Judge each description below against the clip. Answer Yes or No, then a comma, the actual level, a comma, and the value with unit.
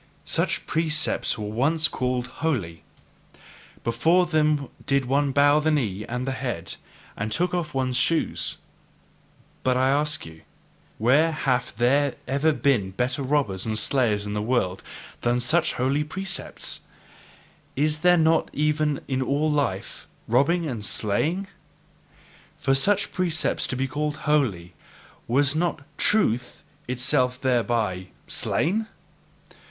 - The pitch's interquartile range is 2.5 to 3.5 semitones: No, average, 4.2 semitones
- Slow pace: Yes, slow, 130 wpm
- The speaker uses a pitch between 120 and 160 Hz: Yes, low, 135 Hz